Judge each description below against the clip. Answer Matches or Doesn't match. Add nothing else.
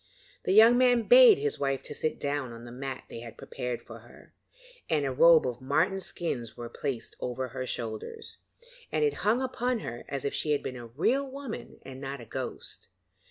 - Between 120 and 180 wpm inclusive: Doesn't match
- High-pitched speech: Doesn't match